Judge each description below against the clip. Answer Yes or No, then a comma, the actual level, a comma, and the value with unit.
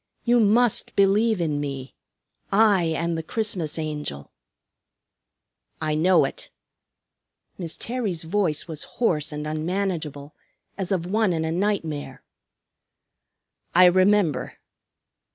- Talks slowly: Yes, slow, 110 wpm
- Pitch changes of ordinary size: Yes, average, 4.7 semitones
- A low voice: No, medium, 170 Hz